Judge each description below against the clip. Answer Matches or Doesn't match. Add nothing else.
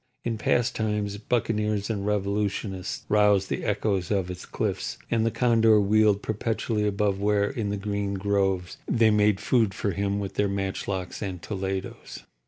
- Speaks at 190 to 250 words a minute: Doesn't match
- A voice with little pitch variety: Matches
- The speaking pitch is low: Matches